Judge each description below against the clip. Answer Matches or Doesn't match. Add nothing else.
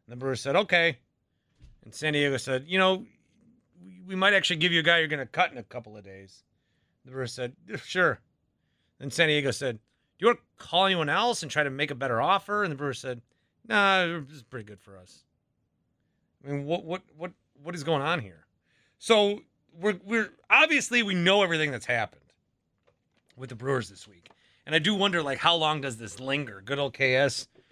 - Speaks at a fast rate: Matches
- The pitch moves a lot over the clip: Matches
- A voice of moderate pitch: Matches